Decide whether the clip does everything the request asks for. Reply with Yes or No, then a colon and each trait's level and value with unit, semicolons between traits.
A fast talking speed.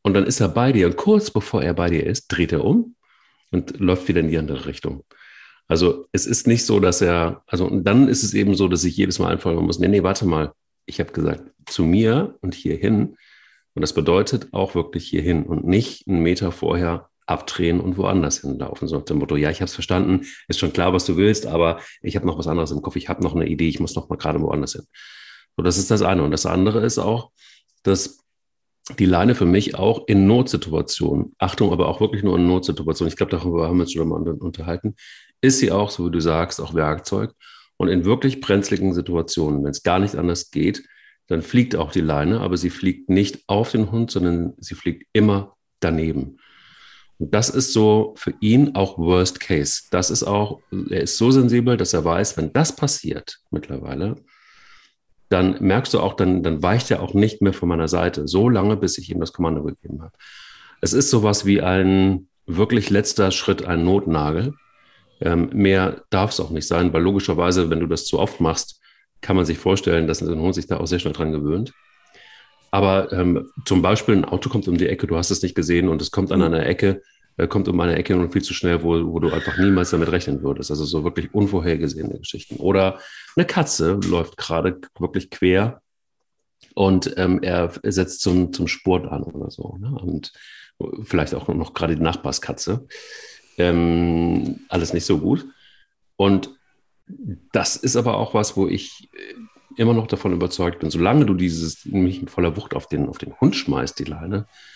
Yes: fast, 205 wpm